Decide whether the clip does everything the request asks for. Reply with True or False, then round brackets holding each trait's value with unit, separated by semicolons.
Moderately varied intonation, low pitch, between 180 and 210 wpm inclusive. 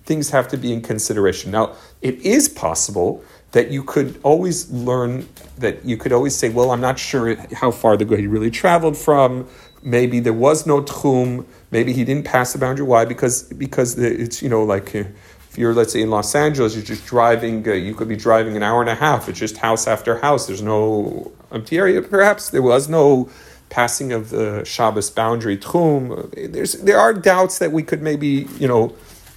True (4.0 semitones; 125 Hz; 200 wpm)